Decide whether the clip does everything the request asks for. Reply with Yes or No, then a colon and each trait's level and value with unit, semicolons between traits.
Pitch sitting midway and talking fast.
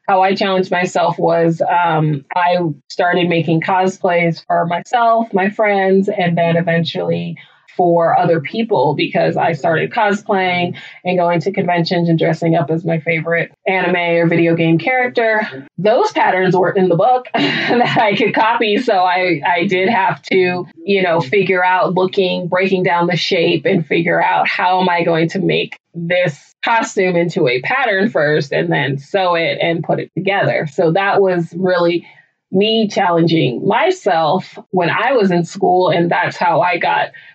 No: medium, 180 Hz; average, 165 wpm